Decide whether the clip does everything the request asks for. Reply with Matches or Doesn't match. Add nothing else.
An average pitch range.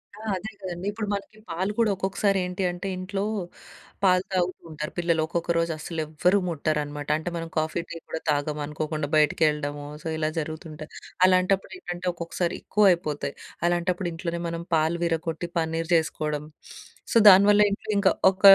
Matches